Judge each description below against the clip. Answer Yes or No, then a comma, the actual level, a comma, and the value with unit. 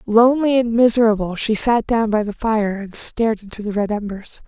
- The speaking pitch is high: Yes, high, 220 Hz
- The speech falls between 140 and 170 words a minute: No, average, 200 wpm